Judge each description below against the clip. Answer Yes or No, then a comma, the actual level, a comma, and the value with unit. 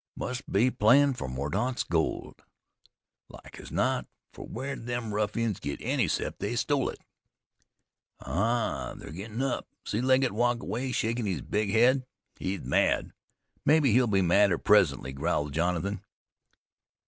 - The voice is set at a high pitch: No, low, 110 Hz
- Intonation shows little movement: No, average, 4.7 semitones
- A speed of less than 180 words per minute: Yes, average, 140 wpm